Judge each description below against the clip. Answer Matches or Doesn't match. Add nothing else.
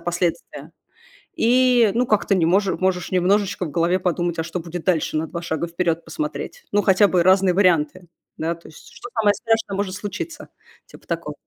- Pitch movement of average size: Matches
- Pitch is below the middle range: Doesn't match